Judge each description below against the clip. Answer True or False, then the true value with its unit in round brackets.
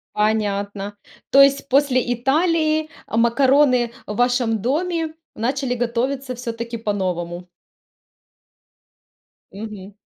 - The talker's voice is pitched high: True (240 Hz)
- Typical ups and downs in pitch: True (4.6 semitones)